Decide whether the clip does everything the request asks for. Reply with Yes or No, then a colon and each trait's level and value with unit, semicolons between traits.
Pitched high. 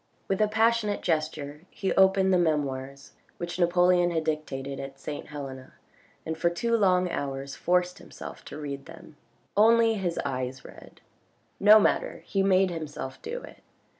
No: medium, 170 Hz